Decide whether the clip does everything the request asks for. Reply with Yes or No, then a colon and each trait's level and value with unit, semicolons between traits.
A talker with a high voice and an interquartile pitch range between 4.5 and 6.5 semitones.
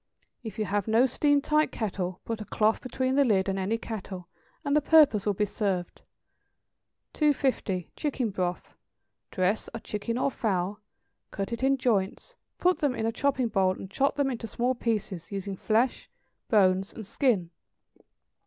Yes: high, 220 Hz; average, 5.0 semitones